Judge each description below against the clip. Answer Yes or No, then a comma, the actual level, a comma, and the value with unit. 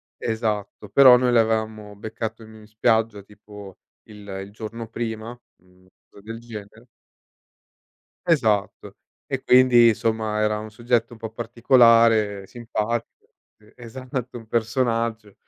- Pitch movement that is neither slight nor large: No, narrow, 1.8 semitones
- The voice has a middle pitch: No, low, 110 Hz